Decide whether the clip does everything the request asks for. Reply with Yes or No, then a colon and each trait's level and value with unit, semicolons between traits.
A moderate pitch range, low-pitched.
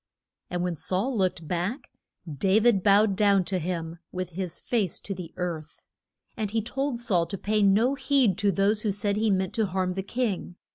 No: average, 3.2 semitones; high, 195 Hz